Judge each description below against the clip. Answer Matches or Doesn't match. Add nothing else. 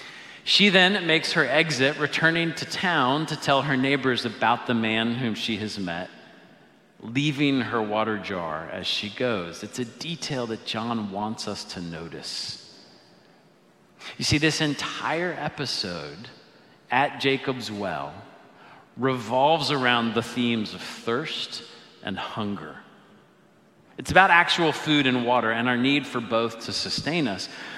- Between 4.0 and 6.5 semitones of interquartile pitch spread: Matches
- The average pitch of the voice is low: Matches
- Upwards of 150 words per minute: Doesn't match